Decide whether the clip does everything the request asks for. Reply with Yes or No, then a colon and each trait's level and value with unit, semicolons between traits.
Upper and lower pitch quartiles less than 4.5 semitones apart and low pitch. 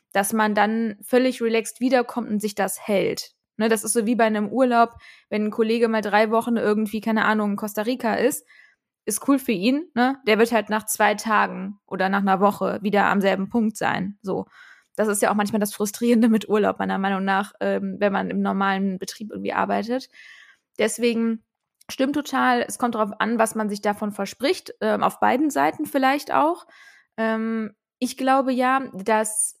No: narrow, 2.5 semitones; high, 220 Hz